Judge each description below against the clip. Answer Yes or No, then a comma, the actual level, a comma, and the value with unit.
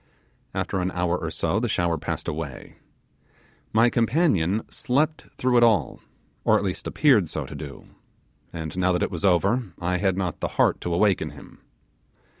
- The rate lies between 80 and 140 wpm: No, average, 175 wpm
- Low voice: Yes, very low, 95 Hz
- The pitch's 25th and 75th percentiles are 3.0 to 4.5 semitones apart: No, average, 5.2 semitones